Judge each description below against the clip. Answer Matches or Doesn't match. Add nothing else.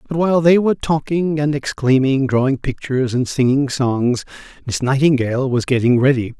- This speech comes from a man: Matches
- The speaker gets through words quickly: Doesn't match